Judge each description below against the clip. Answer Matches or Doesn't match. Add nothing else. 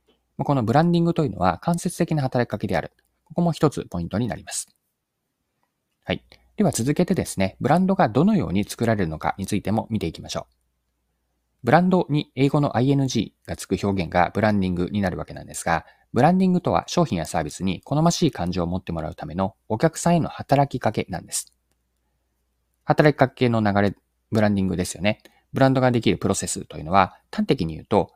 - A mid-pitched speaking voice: Doesn't match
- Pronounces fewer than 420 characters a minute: Doesn't match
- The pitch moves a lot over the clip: Matches